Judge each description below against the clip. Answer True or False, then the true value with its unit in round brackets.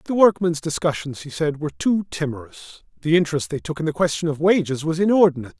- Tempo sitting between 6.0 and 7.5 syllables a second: True (6.9 syllables/s)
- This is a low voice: False (160 Hz)